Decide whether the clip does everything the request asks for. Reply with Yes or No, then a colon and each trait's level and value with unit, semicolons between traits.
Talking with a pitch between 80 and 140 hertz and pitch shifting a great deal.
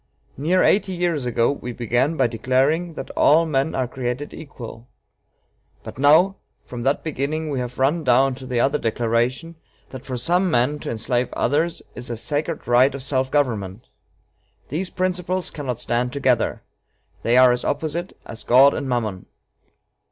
No: low, 135 Hz; average, 4.3 semitones